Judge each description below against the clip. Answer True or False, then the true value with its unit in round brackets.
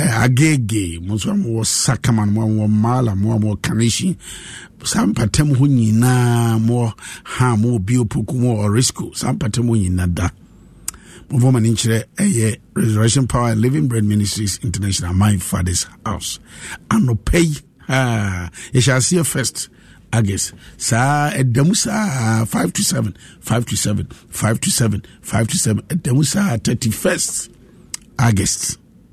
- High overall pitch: False (115 Hz)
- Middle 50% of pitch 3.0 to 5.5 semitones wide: True (3.5 semitones)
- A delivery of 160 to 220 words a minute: False (140 wpm)